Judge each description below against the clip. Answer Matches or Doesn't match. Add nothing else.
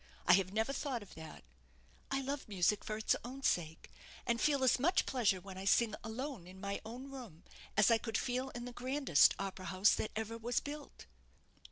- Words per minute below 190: Doesn't match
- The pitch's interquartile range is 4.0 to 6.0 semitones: Matches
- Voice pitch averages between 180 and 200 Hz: Doesn't match